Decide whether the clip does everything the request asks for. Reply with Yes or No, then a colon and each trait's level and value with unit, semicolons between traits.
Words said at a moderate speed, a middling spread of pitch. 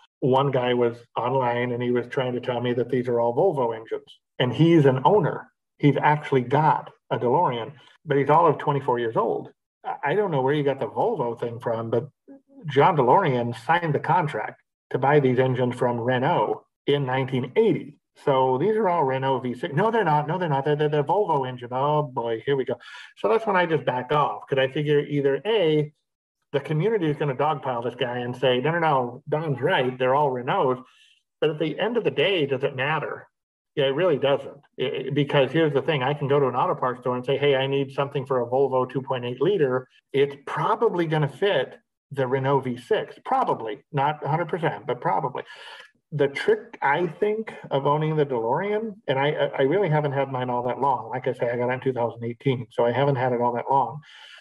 No: fast, 215 wpm; average, 3.1 semitones